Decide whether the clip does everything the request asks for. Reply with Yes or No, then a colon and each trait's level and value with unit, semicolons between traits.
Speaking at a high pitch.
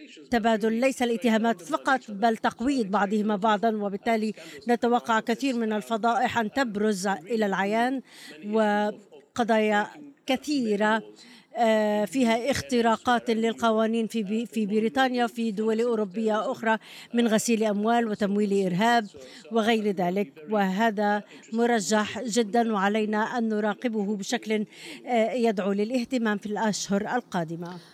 Yes: high, 225 Hz